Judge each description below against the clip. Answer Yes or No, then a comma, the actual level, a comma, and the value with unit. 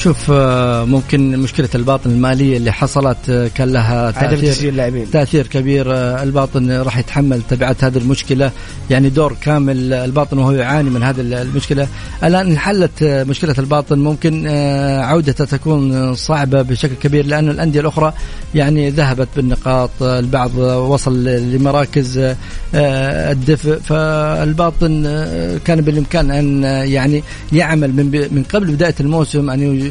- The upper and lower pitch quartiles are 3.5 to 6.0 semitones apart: No, narrow, 2.5 semitones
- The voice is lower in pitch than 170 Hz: Yes, medium, 140 Hz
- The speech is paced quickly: No, average, 120 wpm